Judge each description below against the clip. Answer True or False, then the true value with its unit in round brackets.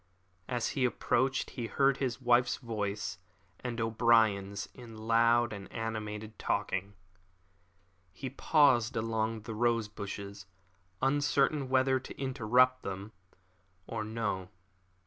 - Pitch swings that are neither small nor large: True (3.0 semitones)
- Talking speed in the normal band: False (110 wpm)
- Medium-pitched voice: False (115 Hz)